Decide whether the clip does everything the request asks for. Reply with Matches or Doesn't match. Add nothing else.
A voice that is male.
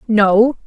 Doesn't match